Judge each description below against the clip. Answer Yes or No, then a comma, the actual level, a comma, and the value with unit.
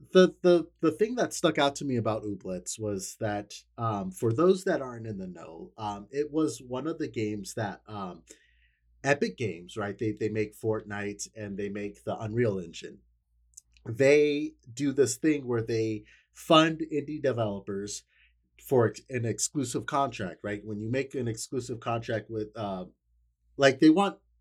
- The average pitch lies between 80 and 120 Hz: Yes, low, 115 Hz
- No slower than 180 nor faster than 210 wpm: No, average, 170 wpm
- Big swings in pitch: Yes, wide, 5.8 semitones